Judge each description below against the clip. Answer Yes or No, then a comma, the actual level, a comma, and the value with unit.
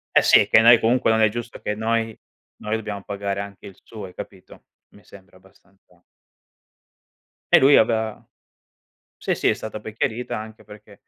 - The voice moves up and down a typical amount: No, narrow, 1.9 semitones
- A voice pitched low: Yes, low, 110 Hz